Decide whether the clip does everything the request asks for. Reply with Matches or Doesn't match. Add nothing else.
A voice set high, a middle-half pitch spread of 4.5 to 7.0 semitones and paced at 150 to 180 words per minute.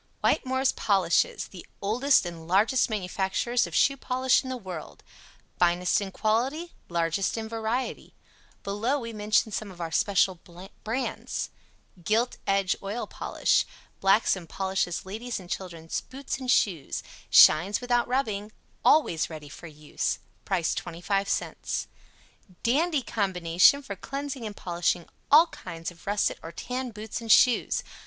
Doesn't match